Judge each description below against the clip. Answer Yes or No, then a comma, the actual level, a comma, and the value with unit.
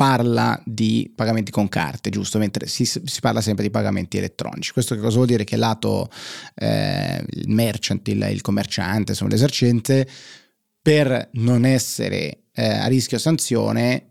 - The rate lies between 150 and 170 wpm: Yes, average, 155 wpm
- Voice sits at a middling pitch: No, low, 115 Hz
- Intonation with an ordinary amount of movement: Yes, average, 3.2 semitones